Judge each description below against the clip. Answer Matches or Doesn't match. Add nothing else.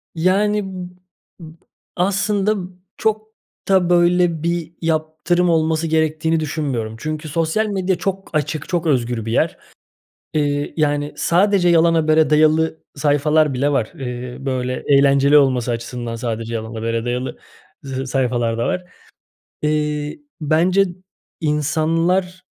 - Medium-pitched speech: Matches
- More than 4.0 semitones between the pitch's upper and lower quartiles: Matches